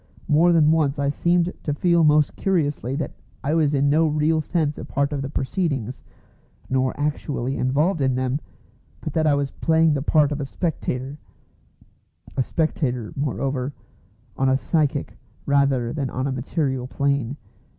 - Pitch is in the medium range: Yes, medium, 145 Hz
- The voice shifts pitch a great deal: No, average, 2.7 semitones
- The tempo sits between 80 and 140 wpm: No, average, 160 wpm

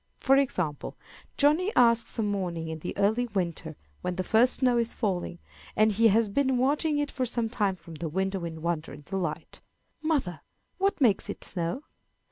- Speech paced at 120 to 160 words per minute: No, average, 180 wpm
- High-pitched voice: Yes, high, 205 Hz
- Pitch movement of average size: No, wide, 6.6 semitones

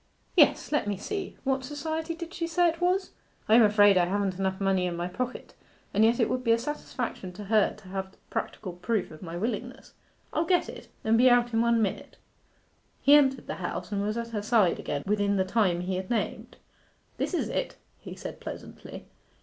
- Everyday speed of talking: No, fast, 210 wpm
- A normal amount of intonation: No, wide, 5.7 semitones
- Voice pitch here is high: Yes, high, 220 Hz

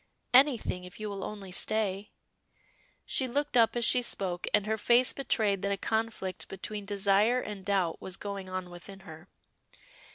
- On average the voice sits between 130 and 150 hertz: No, high, 200 Hz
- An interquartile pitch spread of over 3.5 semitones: No, average, 2.9 semitones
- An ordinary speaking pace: Yes, average, 165 wpm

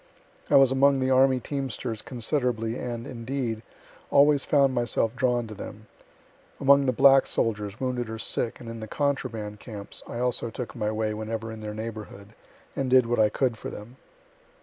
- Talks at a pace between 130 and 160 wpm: No, average, 175 wpm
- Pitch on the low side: Yes, low, 120 Hz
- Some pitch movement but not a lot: Yes, average, 3.2 semitones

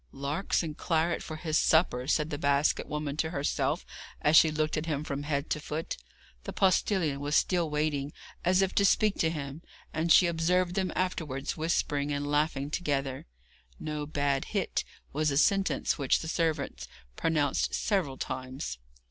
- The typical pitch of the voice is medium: Yes, medium, 155 Hz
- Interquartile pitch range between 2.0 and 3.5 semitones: Yes, average, 2.7 semitones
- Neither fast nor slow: Yes, average, 165 wpm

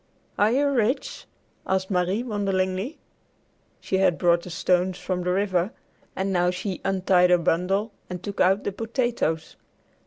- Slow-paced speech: No, average, 150 wpm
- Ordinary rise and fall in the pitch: No, narrow, 2.3 semitones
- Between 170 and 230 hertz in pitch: Yes, high, 190 Hz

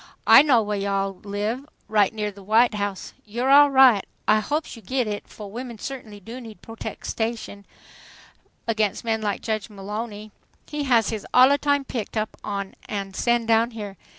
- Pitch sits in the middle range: No, high, 220 Hz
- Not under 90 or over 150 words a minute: No, average, 165 wpm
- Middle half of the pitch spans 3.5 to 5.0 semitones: No, average, 2.8 semitones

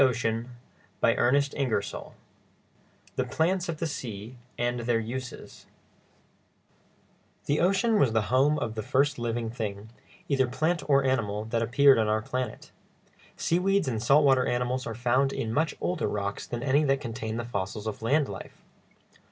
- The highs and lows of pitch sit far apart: No, average, 4.0 semitones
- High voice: No, low, 125 Hz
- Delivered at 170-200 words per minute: No, average, 160 wpm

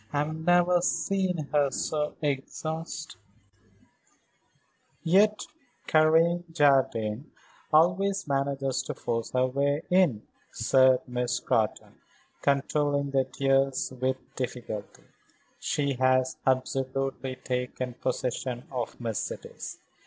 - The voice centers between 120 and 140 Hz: Yes, low, 135 Hz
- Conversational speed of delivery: No, slow, 95 wpm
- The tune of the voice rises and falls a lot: No, average, 3.5 semitones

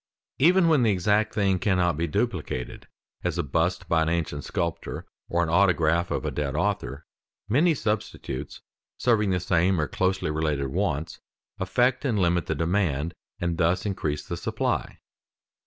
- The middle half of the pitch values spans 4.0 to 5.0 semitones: Yes, average, 4.3 semitones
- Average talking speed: Yes, average, 155 wpm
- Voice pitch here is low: Yes, very low, 85 Hz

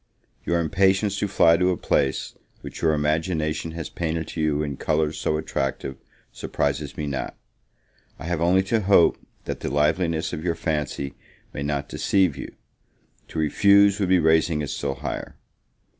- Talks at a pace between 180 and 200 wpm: No, average, 165 wpm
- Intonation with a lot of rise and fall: No, average, 3.3 semitones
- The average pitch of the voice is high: No, very low, 80 Hz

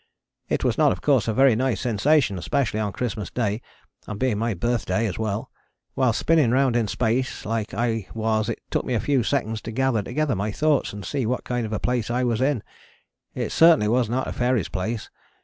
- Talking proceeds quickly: Yes, fast, 215 wpm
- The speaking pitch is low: Yes, low, 115 Hz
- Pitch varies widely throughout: No, average, 3.1 semitones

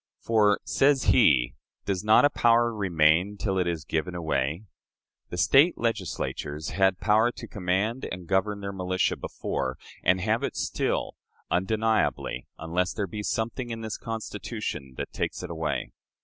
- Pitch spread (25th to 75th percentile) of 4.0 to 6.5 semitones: Yes, average, 4.3 semitones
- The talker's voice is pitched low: Yes, low, 100 Hz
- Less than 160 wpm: Yes, average, 150 wpm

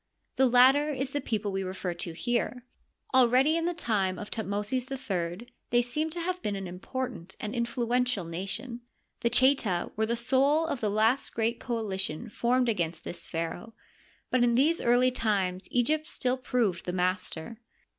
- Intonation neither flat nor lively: Yes, average, 4.9 semitones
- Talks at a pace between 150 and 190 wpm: Yes, average, 165 wpm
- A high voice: Yes, high, 235 Hz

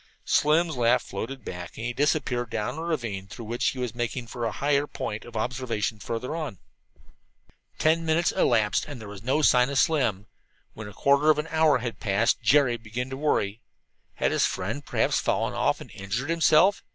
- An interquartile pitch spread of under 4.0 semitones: No, average, 4.9 semitones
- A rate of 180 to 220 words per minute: Yes, average, 190 wpm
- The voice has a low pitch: Yes, low, 125 Hz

